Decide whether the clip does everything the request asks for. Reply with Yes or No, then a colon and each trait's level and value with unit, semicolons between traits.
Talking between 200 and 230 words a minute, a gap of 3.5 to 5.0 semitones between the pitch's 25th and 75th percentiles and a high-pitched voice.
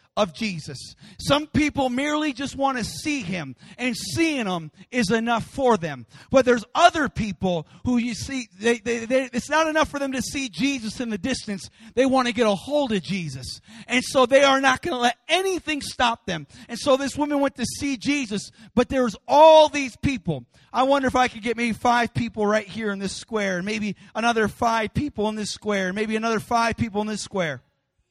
Yes: fast, 205 wpm; average, 4.5 semitones; high, 235 Hz